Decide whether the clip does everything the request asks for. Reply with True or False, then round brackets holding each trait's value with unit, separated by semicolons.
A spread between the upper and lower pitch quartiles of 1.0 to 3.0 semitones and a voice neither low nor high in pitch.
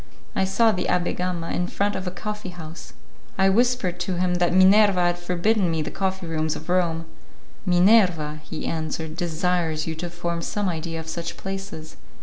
True (2.6 semitones; 175 Hz)